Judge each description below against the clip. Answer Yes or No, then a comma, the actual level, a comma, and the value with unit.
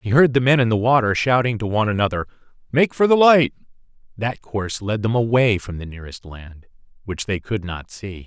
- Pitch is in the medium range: No, low, 115 Hz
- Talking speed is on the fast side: Yes, fast, 210 wpm